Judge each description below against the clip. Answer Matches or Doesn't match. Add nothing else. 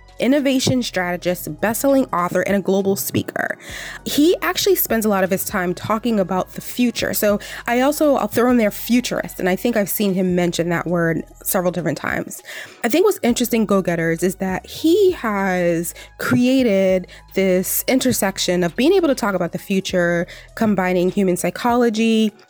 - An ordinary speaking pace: Matches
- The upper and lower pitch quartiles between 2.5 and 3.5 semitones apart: Doesn't match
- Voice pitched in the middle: Doesn't match